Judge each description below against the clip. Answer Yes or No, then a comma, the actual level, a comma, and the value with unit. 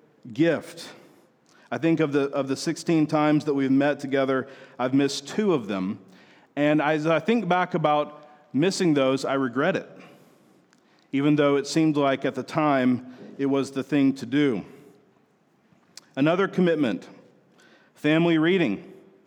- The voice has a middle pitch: Yes, medium, 145 Hz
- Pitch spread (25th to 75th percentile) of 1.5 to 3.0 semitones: Yes, average, 2.7 semitones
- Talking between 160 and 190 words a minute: No, average, 145 wpm